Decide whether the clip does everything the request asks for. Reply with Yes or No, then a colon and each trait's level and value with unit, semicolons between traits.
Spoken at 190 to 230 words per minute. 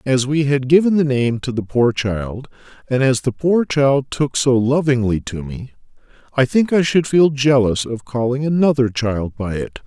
Yes: average, 195 wpm